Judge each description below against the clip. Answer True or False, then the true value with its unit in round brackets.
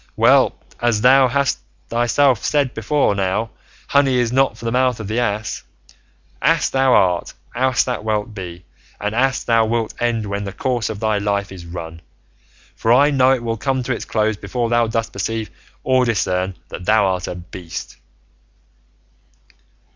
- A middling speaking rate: True (170 wpm)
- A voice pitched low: True (115 Hz)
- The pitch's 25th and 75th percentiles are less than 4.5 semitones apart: True (3.7 semitones)